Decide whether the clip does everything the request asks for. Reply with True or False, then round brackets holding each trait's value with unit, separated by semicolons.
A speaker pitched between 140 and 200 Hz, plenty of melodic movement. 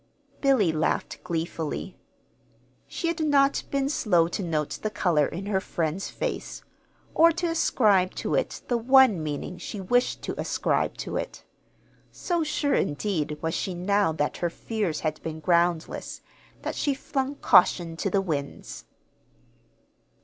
True (190 Hz; 8.3 semitones)